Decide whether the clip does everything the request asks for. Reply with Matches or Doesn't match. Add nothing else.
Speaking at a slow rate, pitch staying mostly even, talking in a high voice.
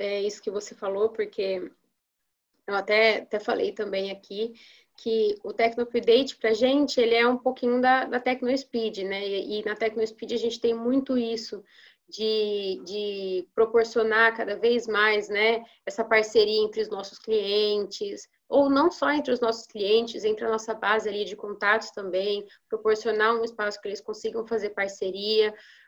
Doesn't match